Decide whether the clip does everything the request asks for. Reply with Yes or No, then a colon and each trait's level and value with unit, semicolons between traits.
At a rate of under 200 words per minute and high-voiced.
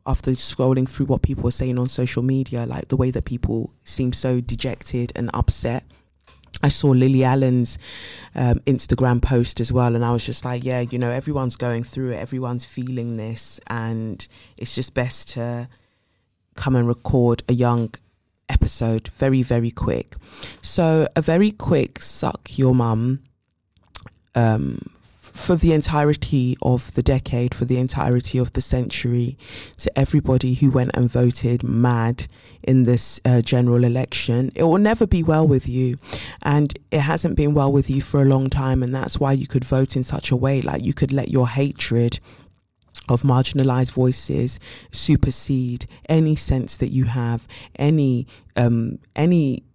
No: average, 165 wpm; low, 125 Hz